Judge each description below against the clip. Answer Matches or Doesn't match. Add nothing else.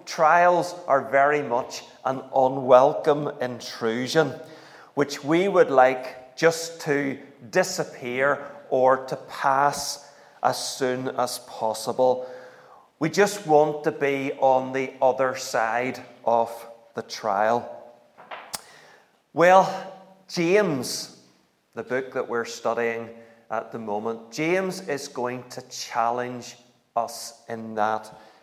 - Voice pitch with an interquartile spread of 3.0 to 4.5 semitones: Matches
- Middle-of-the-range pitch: Doesn't match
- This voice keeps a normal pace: Doesn't match